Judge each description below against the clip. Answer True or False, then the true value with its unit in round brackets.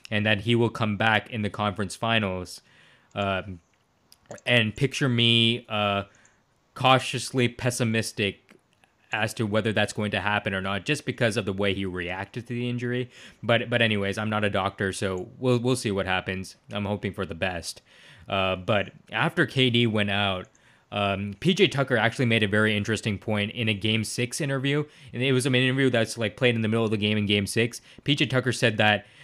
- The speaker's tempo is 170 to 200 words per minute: True (195 wpm)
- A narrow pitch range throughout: False (3.3 semitones)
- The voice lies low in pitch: True (110 Hz)